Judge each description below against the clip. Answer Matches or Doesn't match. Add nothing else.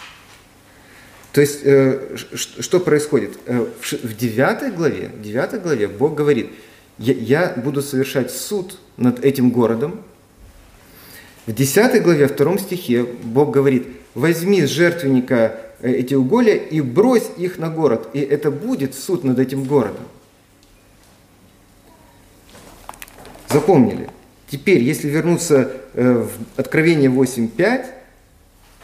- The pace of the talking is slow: Matches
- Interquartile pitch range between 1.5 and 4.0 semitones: Doesn't match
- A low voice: Matches